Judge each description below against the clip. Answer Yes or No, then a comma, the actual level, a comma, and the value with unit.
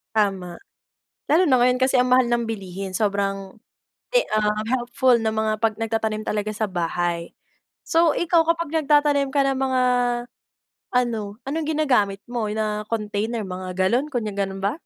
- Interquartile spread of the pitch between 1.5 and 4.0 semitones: No, average, 4.5 semitones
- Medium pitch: No, high, 220 Hz